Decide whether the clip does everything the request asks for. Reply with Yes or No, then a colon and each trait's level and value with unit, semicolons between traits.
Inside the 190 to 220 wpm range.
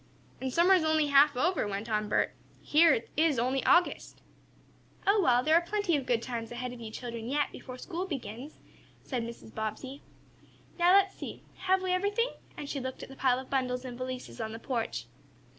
Yes: average, 200 wpm